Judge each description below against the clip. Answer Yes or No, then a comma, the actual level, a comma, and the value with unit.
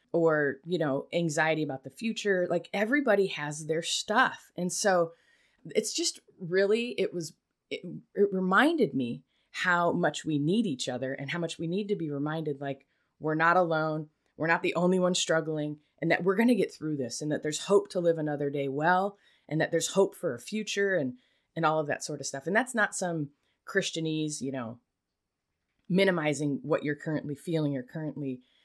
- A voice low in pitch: No, medium, 165 Hz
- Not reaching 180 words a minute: No, average, 195 wpm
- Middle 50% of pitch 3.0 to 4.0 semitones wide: No, average, 4.4 semitones